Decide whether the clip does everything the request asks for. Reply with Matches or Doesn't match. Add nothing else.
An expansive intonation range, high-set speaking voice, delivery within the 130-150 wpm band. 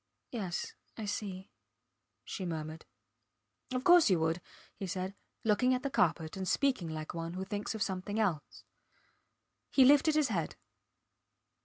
Matches